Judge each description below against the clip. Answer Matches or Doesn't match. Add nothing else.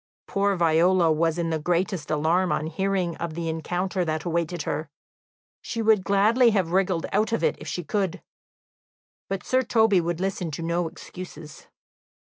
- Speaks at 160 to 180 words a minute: Matches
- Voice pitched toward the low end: Doesn't match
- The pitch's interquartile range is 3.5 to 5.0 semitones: Doesn't match